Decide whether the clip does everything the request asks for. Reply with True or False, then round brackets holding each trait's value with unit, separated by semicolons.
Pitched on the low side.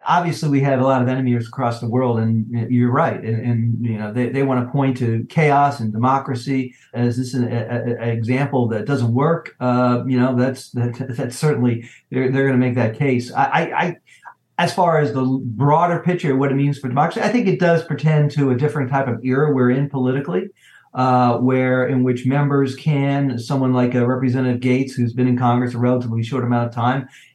True (130 Hz)